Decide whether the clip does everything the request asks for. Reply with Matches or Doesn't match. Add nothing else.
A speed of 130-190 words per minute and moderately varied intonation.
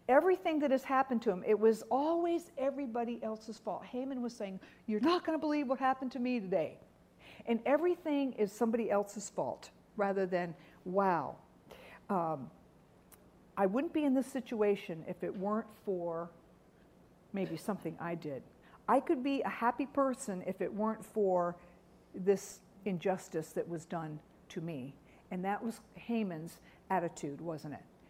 Doesn't match